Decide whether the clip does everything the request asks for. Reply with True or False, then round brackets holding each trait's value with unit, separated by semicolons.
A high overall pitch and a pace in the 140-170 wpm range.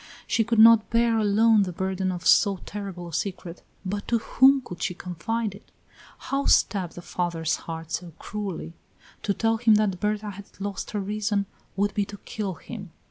False (200 Hz; 185 wpm)